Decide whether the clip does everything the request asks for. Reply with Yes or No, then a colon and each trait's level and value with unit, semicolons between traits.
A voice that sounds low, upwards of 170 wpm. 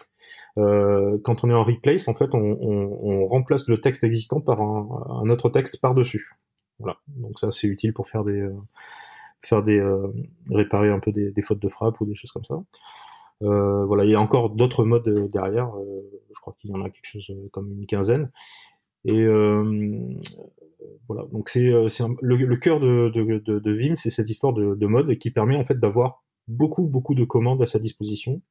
Yes: low, 110 Hz; average, 210 wpm